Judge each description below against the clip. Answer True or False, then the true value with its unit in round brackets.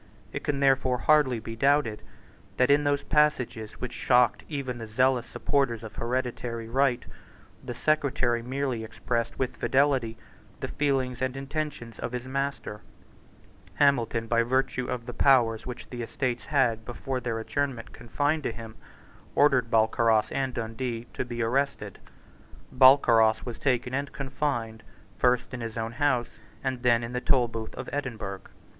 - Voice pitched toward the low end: True (125 Hz)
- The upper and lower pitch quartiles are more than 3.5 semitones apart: False (2.8 semitones)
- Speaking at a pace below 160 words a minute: True (150 wpm)